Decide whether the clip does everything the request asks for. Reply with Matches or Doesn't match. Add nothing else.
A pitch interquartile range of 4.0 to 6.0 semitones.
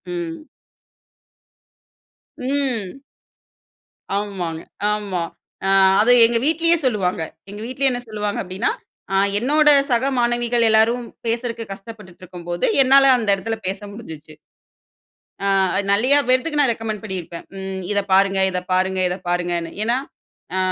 Matches